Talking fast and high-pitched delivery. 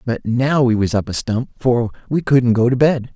No: fast, 245 wpm; low, 120 Hz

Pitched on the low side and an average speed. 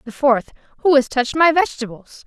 No: very high, 270 Hz; average, 185 wpm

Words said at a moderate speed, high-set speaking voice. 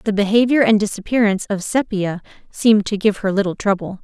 Yes: average, 180 wpm; high, 205 Hz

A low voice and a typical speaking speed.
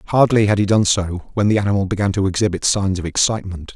No: low, 100 Hz; fast, 225 wpm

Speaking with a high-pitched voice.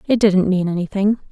Yes: high, 195 Hz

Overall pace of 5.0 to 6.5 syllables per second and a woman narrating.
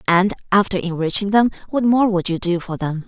Yes: 5.5 syllables/s; female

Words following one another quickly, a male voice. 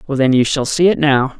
Yes: fast, 300 wpm; male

